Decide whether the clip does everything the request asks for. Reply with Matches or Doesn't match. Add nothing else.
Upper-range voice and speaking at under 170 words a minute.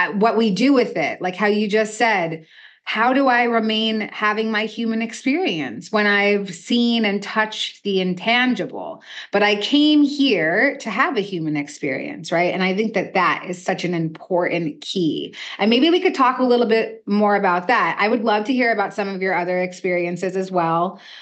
Doesn't match